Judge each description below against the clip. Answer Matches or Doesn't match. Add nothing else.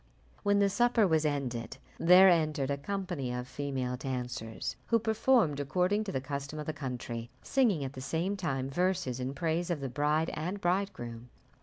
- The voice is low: Doesn't match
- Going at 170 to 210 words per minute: Matches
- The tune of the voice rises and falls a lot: Matches